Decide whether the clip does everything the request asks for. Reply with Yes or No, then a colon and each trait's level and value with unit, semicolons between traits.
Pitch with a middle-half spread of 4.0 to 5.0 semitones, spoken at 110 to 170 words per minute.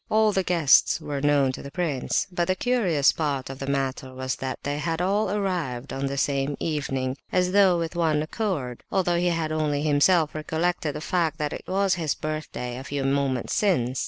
No: average, 4.5 semitones; average, 200 wpm